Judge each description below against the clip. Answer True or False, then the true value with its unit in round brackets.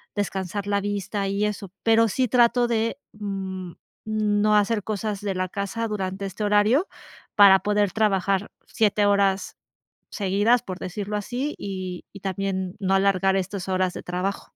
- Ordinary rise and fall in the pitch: False (1.7 semitones)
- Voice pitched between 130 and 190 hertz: False (200 Hz)